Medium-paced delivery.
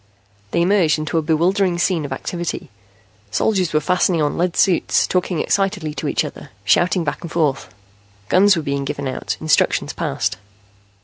Yes: average, 165 wpm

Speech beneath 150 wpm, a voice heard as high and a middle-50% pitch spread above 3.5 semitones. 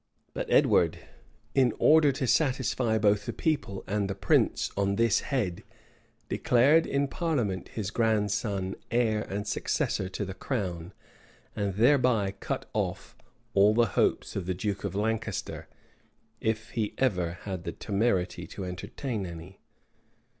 No: average, 140 wpm; low, 105 Hz; average, 3.9 semitones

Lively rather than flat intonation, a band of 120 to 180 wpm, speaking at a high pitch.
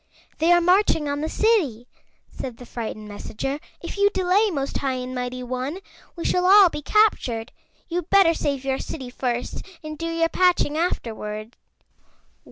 Yes: wide, 6.2 semitones; average, 165 wpm; very high, 295 Hz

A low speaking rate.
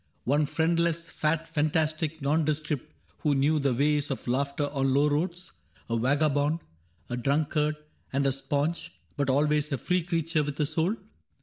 No: average, 160 wpm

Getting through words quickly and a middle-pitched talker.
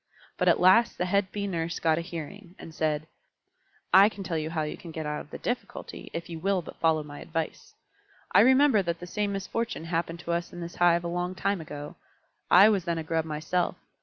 Yes: fast, 225 wpm; medium, 170 Hz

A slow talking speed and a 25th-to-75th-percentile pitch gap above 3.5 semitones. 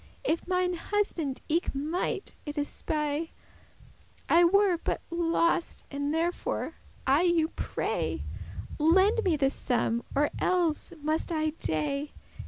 No: slow, 125 wpm; average, 3.2 semitones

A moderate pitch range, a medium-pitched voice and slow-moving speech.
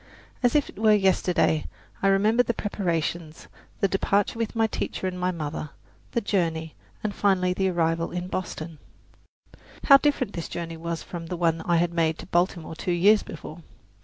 No: average, 3.5 semitones; medium, 180 Hz; average, 175 wpm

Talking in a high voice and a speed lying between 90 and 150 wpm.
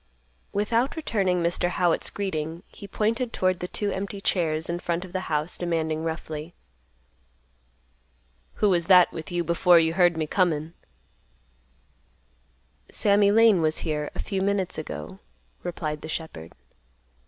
No: medium, 175 Hz; average, 140 wpm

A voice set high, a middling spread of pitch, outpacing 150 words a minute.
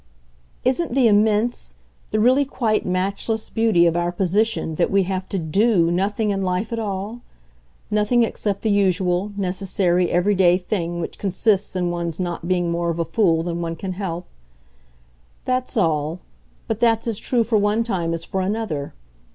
Yes: high, 195 Hz; average, 3.9 semitones; average, 170 wpm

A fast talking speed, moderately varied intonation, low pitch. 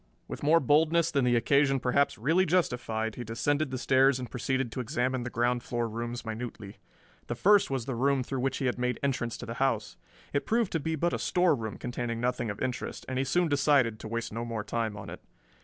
Yes: fast, 225 wpm; average, 3.2 semitones; low, 125 Hz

